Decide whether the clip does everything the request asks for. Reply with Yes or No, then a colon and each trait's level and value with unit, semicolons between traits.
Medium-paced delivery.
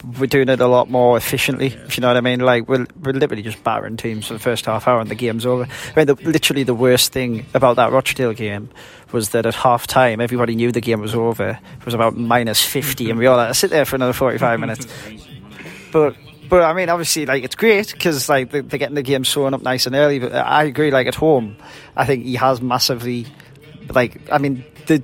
No: fast, 245 wpm